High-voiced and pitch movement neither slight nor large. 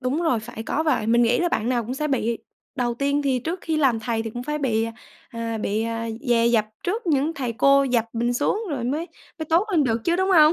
Yes: very high, 255 Hz; average, 4.9 semitones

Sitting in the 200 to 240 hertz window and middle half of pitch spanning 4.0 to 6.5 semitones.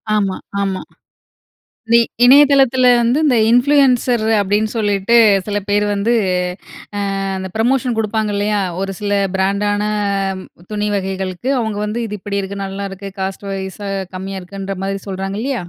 No: high, 205 Hz; average, 3.2 semitones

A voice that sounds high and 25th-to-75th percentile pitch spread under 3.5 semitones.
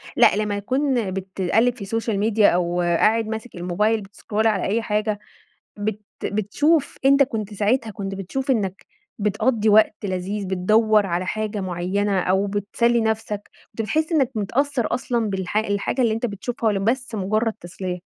Yes: high, 210 Hz; average, 2.7 semitones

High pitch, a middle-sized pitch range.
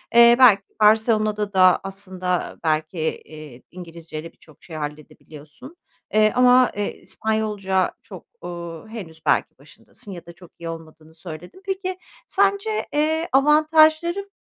No: high, 195 Hz; wide, 7.5 semitones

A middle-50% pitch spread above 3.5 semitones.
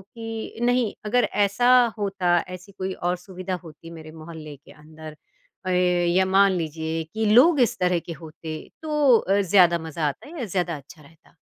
Yes: average, 4.4 semitones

